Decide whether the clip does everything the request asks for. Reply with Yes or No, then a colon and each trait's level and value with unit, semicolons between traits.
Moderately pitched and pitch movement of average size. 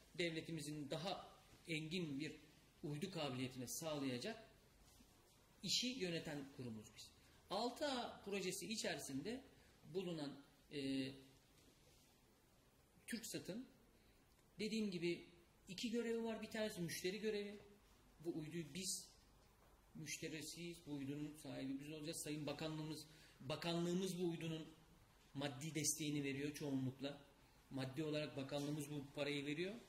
Yes: medium, 155 Hz; average, 4.2 semitones